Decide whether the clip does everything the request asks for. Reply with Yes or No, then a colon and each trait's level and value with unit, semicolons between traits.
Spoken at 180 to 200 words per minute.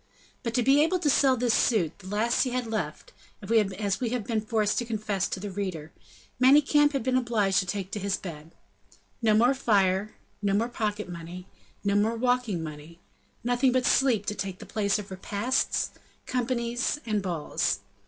Yes: average, 185 wpm